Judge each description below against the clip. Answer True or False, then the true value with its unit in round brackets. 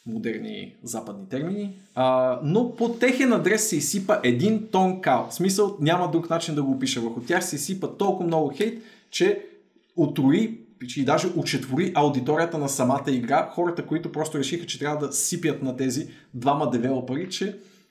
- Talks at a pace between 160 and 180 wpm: True (165 wpm)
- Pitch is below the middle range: False (160 Hz)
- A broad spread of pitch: True (6.5 semitones)